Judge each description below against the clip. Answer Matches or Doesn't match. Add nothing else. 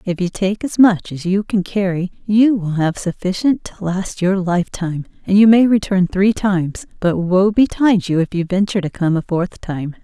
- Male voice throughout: Doesn't match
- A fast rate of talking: Matches